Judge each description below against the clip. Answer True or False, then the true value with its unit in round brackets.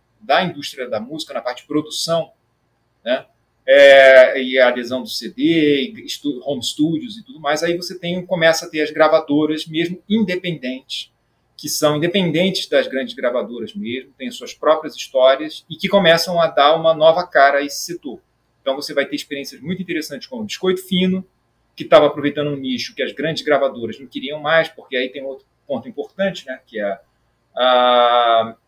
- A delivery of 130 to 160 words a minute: False (180 wpm)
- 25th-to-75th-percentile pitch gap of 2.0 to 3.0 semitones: False (5.1 semitones)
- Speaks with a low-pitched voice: False (150 Hz)